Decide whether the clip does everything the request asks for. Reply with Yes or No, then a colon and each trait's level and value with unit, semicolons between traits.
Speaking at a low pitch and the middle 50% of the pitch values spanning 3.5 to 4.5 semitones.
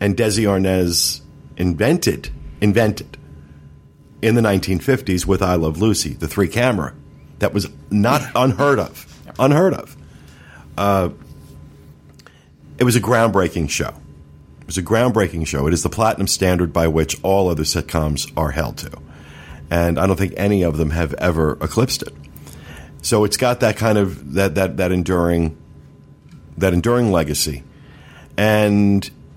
No: very low, 90 Hz; average, 5.1 semitones